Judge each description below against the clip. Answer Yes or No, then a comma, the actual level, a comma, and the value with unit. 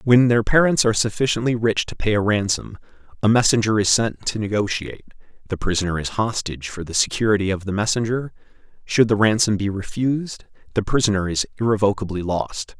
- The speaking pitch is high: No, low, 105 Hz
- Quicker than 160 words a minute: Yes, average, 170 wpm